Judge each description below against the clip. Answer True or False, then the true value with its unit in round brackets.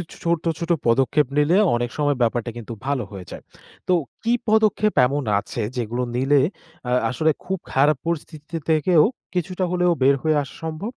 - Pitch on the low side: False (150 Hz)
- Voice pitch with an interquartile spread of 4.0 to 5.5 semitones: True (5.1 semitones)